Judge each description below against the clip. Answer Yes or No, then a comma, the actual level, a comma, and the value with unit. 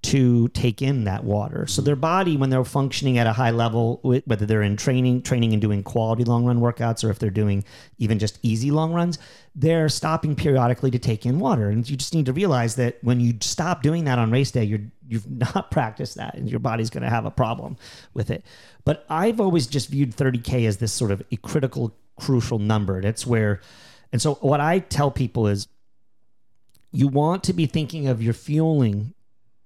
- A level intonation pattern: No, average, 4.0 semitones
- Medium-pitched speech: No, low, 120 Hz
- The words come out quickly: Yes, fast, 210 wpm